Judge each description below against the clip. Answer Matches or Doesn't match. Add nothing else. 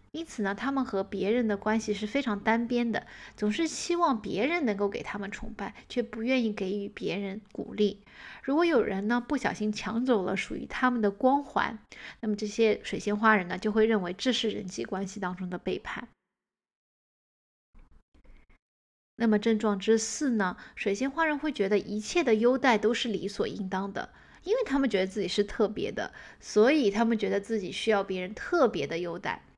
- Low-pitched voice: Doesn't match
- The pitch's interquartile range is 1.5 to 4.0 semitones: Matches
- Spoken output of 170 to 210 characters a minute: Doesn't match